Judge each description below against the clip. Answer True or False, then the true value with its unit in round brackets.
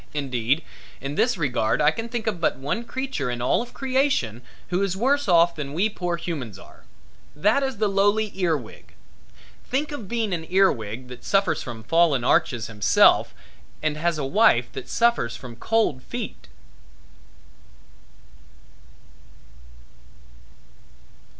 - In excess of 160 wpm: False (140 wpm)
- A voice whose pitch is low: False (170 Hz)